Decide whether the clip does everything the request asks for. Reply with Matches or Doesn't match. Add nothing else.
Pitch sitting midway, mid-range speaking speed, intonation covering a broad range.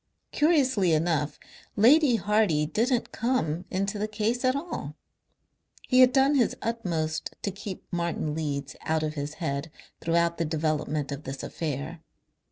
Matches